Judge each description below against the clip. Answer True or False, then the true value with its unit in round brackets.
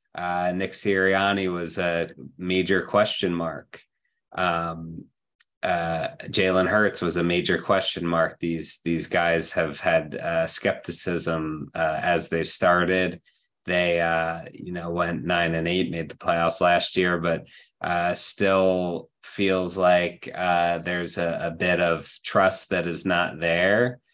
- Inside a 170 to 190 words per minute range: False (140 wpm)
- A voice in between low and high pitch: False (85 Hz)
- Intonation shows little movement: True (1.7 semitones)